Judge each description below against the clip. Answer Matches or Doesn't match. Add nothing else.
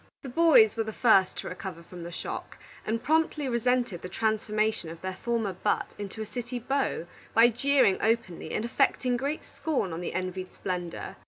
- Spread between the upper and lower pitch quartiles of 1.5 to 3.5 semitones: Doesn't match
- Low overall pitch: Doesn't match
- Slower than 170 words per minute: Doesn't match